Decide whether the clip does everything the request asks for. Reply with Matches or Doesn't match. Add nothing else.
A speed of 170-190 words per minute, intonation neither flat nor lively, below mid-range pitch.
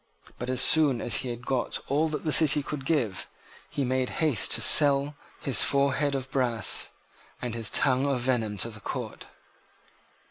Matches